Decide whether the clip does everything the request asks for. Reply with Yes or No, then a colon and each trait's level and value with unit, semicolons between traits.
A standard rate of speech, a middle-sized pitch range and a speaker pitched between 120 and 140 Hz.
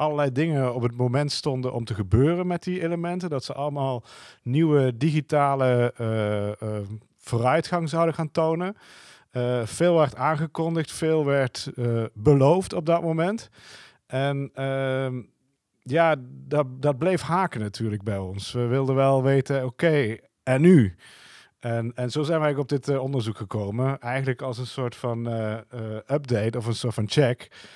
Yes: average, 160 wpm; average, 4.3 semitones; low, 135 Hz